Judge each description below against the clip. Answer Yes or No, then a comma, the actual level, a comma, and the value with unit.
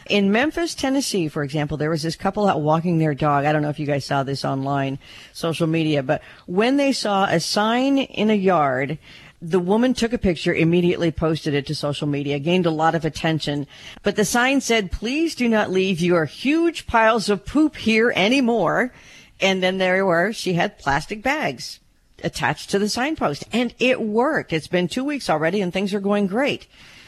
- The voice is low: No, medium, 185 Hz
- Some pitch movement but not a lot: No, wide, 6.4 semitones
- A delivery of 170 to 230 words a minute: Yes, average, 195 wpm